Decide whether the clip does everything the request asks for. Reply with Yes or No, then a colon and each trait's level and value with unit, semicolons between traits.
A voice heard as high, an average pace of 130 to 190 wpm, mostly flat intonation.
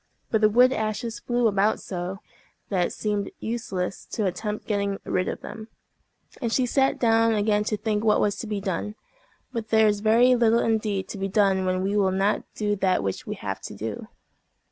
No: high, 210 Hz; average, 200 wpm; narrow, 2.3 semitones